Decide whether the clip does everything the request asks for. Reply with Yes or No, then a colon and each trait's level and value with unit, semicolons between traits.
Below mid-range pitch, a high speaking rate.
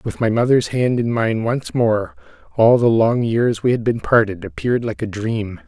Yes: low, 115 Hz; fast, 210 wpm